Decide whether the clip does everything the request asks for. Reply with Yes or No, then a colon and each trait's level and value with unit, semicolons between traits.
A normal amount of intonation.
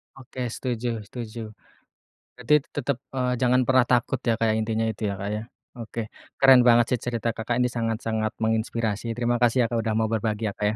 No: narrow, 2.0 semitones